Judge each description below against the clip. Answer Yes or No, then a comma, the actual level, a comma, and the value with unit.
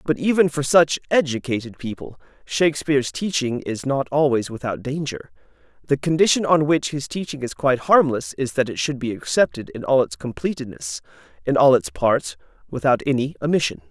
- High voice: No, low, 135 Hz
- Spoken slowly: No, average, 170 wpm